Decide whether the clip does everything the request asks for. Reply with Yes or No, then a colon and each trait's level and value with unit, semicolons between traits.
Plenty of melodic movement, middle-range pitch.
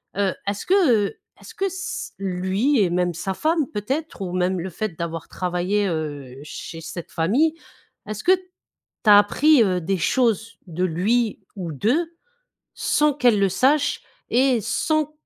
No: wide, 6.9 semitones; high, 205 Hz